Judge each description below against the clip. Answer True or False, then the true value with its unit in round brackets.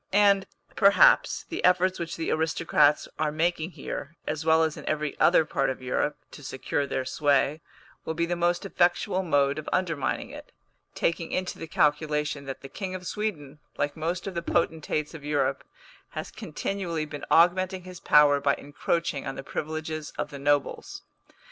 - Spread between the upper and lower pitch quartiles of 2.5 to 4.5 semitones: True (3.2 semitones)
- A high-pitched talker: False (155 Hz)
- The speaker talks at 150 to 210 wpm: True (175 wpm)